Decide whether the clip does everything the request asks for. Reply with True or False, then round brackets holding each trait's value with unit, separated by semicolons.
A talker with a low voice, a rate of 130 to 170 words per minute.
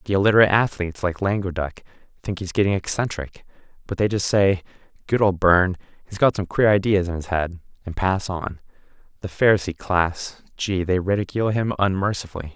True (95 Hz; 160 wpm)